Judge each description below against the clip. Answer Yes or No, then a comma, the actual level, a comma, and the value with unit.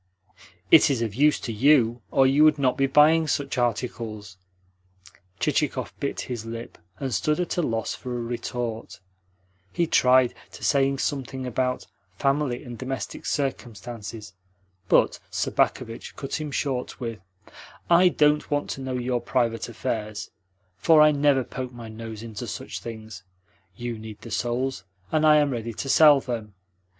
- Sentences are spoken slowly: No, average, 155 wpm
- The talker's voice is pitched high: No, low, 125 Hz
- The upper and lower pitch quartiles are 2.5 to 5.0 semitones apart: Yes, average, 3.6 semitones